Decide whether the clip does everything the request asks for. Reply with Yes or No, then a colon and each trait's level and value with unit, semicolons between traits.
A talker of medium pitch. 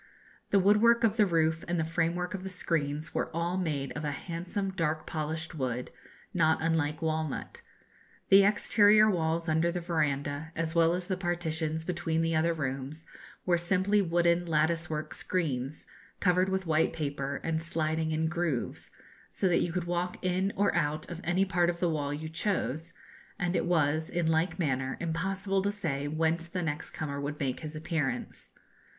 Yes: medium, 165 Hz